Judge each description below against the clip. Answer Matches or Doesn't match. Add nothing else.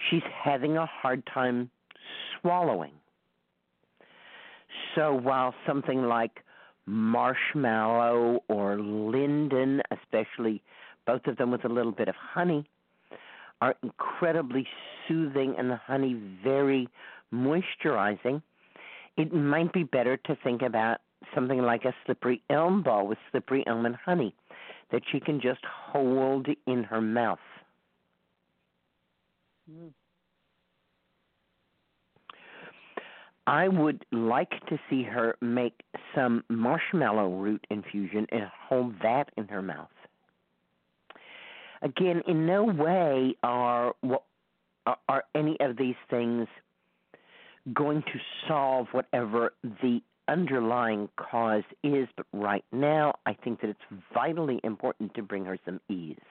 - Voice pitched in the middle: Doesn't match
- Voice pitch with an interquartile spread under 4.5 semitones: Doesn't match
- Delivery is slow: Matches